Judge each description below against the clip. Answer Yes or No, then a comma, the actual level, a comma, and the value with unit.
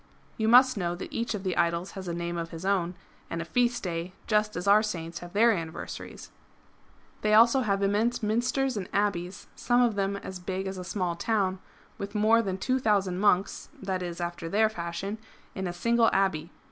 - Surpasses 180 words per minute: Yes, average, 195 wpm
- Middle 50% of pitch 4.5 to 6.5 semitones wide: No, average, 3.7 semitones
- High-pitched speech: Yes, high, 195 Hz